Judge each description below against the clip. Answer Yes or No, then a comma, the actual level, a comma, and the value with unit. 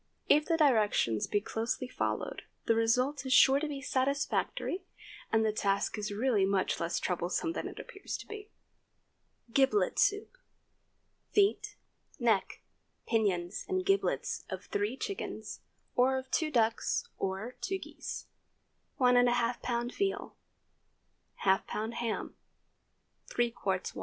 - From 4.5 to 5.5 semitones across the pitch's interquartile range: Yes, average, 5.1 semitones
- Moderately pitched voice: No, high, 245 Hz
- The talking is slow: Yes, slow, 125 wpm